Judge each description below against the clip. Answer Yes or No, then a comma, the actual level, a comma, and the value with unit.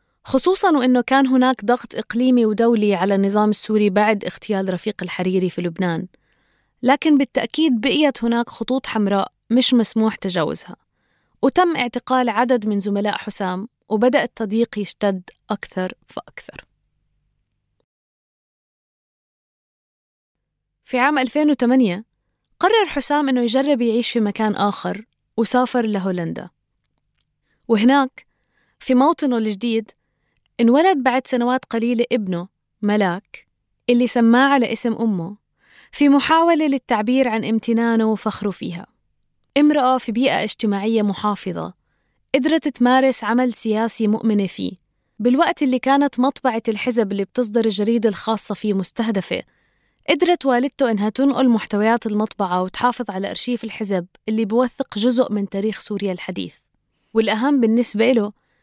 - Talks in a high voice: Yes, high, 230 Hz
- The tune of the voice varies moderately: Yes, average, 3.6 semitones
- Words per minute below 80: No, average, 115 wpm